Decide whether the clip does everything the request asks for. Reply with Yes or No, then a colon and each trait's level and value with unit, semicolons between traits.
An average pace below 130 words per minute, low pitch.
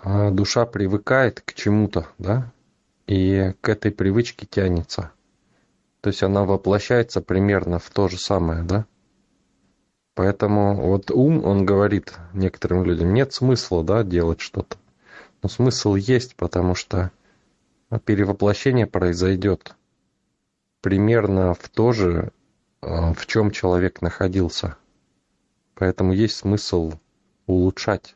Yes: slow, 110 wpm; low, 100 Hz